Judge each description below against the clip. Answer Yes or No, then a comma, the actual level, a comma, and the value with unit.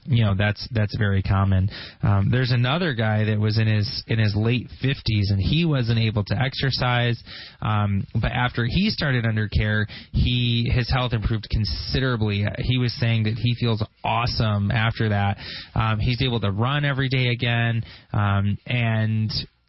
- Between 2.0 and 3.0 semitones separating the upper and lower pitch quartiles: Yes, average, 2.7 semitones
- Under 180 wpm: Yes, average, 170 wpm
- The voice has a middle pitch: No, low, 115 Hz